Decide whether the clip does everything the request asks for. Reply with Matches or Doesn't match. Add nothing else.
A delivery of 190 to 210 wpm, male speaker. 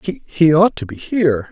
Matches